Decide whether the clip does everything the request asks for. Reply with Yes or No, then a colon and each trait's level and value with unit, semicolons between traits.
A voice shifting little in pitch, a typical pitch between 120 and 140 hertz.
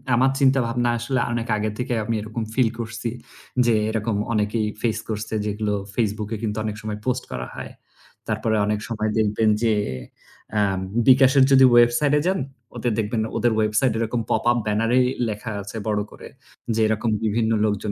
No: narrow, 2.0 semitones; low, 110 Hz